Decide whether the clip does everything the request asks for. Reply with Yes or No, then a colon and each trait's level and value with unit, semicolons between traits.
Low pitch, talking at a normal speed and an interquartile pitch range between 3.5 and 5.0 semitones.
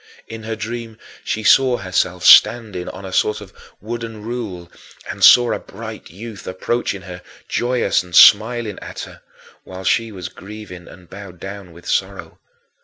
Yes: low, 105 Hz; average, 160 wpm; average, 3.8 semitones